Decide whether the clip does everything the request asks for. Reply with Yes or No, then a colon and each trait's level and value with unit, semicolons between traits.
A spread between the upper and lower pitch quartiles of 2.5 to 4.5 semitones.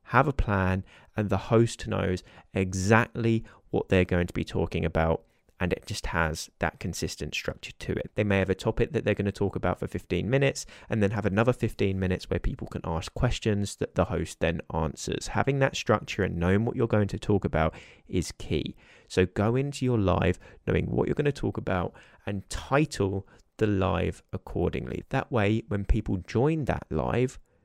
Yes: average, 3.7 semitones